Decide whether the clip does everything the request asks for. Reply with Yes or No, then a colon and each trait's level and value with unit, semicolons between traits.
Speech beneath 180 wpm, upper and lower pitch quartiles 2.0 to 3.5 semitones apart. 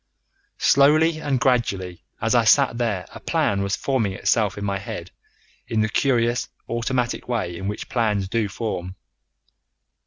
No: average, 150 wpm; average, 3.9 semitones